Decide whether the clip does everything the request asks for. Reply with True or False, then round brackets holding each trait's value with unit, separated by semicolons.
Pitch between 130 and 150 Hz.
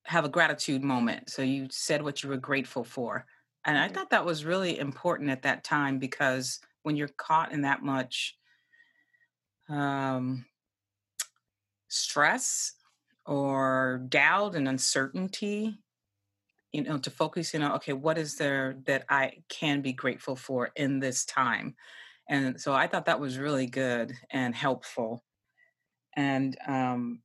True (135 Hz)